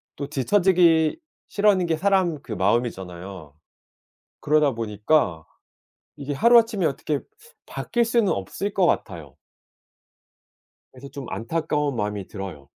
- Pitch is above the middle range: No, medium, 140 Hz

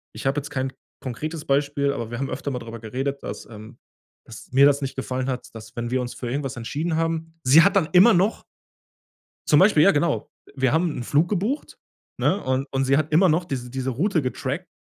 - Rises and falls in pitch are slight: No, average, 4.0 semitones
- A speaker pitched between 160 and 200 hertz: No, medium, 140 Hz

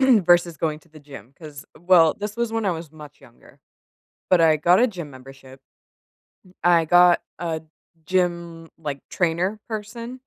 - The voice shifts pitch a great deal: No, average, 3.5 semitones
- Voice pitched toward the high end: No, medium, 170 Hz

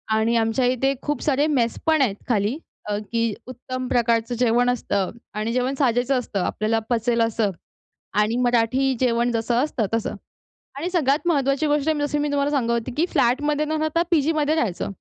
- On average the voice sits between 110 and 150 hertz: No, very high, 250 Hz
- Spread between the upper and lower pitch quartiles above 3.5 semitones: Yes, average, 3.9 semitones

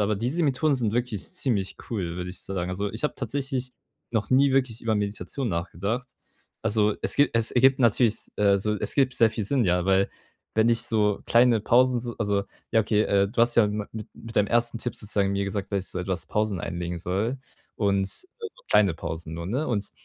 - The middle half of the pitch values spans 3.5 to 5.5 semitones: Yes, average, 3.8 semitones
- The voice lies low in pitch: Yes, low, 110 Hz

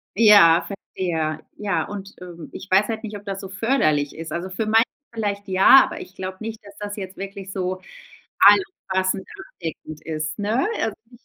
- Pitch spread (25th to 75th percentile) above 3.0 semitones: No, average, 2.7 semitones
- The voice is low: No, high, 195 Hz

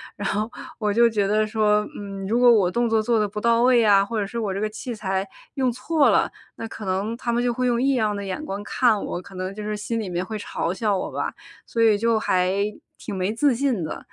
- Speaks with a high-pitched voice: Yes, high, 215 Hz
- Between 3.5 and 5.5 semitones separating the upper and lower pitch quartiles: No, average, 2.9 semitones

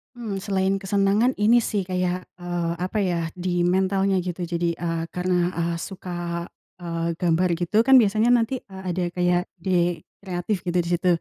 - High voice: No, medium, 180 Hz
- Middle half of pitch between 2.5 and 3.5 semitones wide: No, narrow, 2.1 semitones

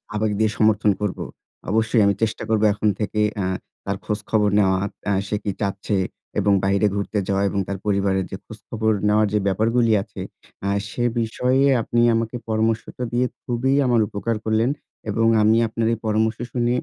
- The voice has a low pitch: Yes, low, 110 Hz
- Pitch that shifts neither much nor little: No, narrow, 1.9 semitones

